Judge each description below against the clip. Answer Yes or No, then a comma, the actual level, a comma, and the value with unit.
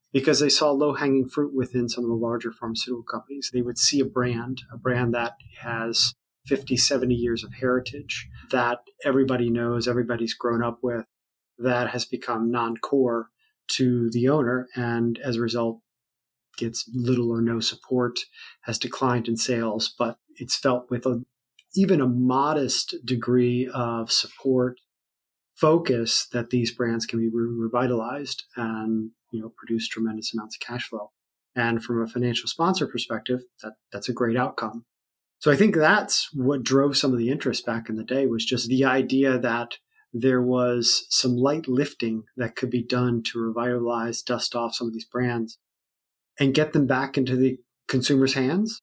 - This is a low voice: Yes, low, 125 Hz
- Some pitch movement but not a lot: No, narrow, 1.9 semitones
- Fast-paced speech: No, average, 165 wpm